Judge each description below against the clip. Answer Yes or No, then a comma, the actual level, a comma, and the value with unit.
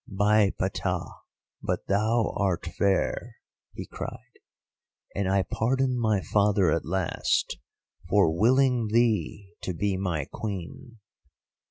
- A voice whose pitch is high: No, low, 100 Hz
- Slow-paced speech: Yes, slow, 115 wpm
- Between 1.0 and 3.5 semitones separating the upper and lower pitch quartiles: Yes, average, 2.9 semitones